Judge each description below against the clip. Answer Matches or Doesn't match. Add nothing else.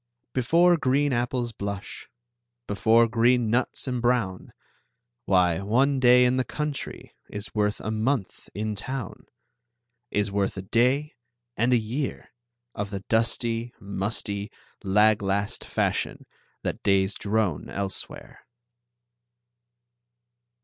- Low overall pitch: Matches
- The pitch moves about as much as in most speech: Matches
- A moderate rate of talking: Doesn't match